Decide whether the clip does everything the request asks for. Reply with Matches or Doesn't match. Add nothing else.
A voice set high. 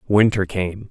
Doesn't match